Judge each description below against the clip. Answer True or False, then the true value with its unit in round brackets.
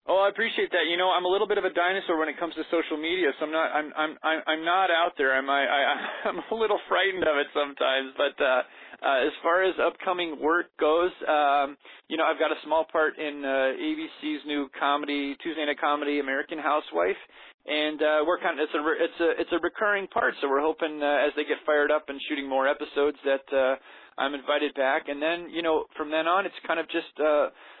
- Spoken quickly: True (235 wpm)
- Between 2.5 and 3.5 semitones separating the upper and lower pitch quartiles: True (2.9 semitones)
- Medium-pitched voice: True (155 Hz)